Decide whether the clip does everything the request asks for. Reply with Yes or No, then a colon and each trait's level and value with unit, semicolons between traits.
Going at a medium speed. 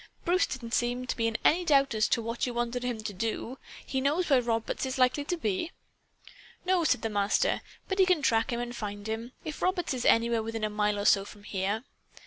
No: fast, 230 wpm